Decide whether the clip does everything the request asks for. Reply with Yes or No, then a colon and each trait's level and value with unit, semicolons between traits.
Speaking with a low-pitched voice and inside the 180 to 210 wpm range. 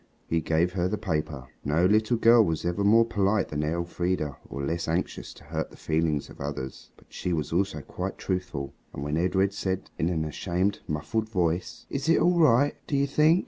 Yes: very low, 90 Hz; average, 200 wpm